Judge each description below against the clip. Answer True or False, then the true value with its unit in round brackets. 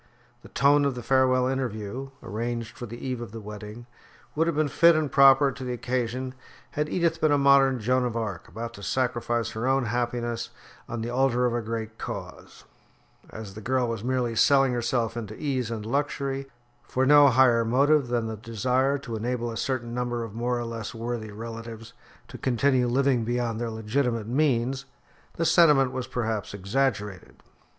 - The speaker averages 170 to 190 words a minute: True (180 wpm)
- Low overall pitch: True (120 Hz)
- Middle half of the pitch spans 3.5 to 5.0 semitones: False (2.7 semitones)